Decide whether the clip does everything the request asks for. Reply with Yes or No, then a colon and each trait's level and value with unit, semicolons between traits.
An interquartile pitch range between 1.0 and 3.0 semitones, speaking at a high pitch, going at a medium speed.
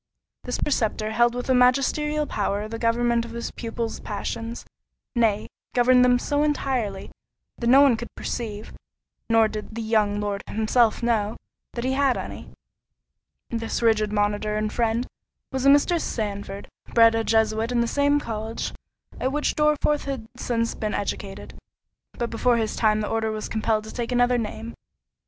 Yes: narrow, 2.4 semitones; high, 230 Hz; average, 165 wpm